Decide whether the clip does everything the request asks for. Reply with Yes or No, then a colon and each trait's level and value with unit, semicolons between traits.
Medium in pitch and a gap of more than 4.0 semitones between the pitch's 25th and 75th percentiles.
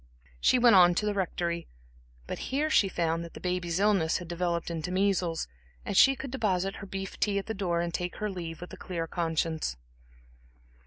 No: medium, 180 Hz; average, 2.8 semitones